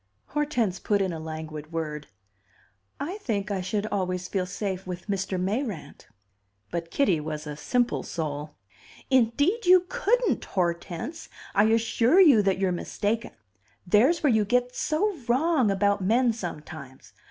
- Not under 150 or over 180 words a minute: No, average, 140 wpm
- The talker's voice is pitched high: Yes, high, 200 Hz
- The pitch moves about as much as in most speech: No, wide, 6.4 semitones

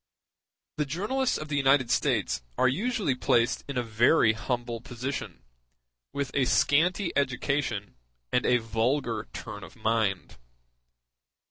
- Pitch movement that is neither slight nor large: Yes, average, 4.1 semitones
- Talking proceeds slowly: Yes, slow, 125 wpm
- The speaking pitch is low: Yes, low, 130 Hz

